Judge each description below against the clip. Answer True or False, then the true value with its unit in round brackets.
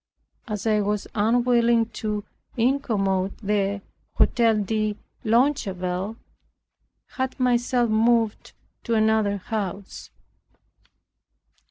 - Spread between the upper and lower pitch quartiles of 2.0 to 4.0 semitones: True (2.7 semitones)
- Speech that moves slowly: True (85 wpm)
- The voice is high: True (220 Hz)